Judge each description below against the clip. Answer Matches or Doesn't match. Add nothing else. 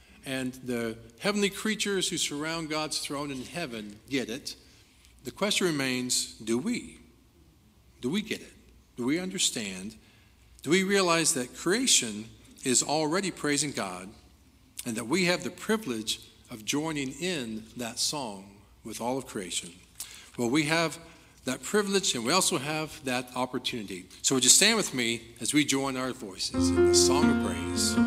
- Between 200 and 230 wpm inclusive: Doesn't match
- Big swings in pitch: Matches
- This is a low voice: Matches